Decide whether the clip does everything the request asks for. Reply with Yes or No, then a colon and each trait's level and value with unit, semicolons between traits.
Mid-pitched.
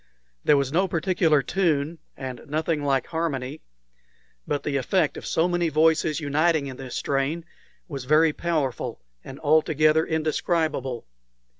Yes: medium, 155 Hz